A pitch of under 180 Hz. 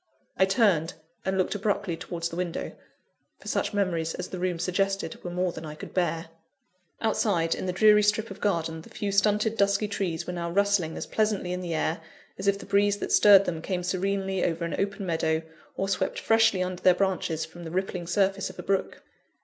No: medium, 185 Hz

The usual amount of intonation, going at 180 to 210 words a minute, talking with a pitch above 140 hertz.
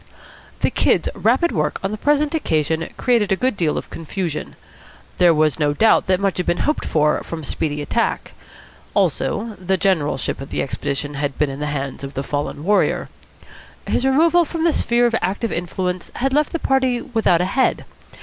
No: wide, 8.3 semitones; average, 190 wpm; medium, 185 Hz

